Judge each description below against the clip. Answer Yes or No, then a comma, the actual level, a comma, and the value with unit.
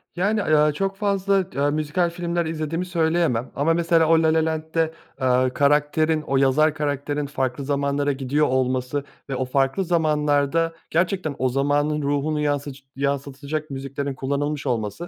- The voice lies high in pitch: No, medium, 150 Hz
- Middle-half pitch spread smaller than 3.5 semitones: Yes, average, 2.8 semitones